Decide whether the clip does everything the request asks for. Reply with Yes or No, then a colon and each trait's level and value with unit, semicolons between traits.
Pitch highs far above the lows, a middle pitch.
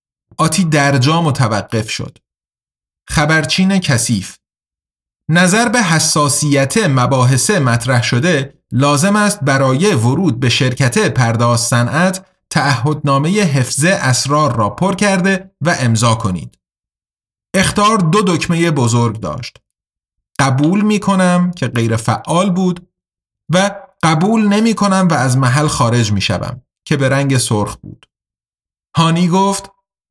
Yes: wide, 7.0 semitones; medium, 145 Hz